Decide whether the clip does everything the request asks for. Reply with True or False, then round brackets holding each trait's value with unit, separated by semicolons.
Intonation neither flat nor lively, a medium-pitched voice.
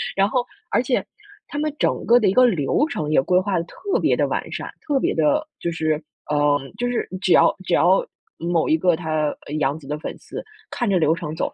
False (7.6 semitones; 175 Hz)